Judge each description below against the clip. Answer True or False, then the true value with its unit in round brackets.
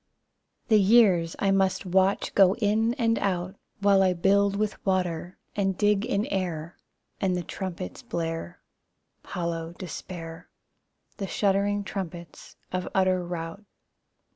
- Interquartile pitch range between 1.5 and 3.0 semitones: True (2.6 semitones)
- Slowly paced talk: True (125 wpm)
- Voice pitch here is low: False (190 Hz)